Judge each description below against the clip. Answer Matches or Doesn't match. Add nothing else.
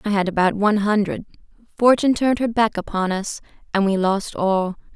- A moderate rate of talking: Matches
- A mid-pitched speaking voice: Doesn't match